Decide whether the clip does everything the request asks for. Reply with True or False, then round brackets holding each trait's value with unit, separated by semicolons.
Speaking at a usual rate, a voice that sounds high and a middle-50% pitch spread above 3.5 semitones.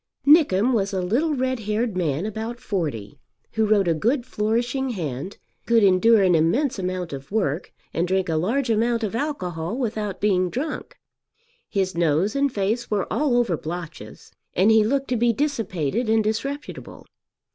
True (165 wpm; 210 Hz; 4.9 semitones)